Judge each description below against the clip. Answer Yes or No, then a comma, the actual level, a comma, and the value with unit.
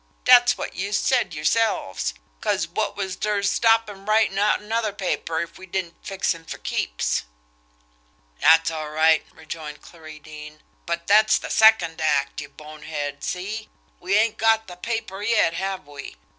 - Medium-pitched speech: Yes, medium, 180 Hz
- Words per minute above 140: Yes, average, 160 wpm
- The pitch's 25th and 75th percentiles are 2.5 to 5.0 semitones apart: No, wide, 5.4 semitones